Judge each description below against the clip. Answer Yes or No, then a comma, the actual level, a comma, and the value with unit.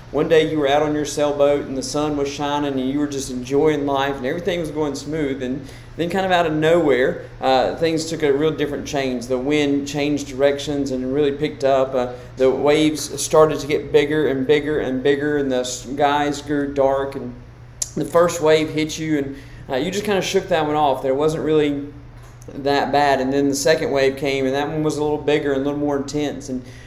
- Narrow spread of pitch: Yes, narrow, 2.1 semitones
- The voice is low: No, medium, 145 Hz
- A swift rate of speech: Yes, fast, 230 wpm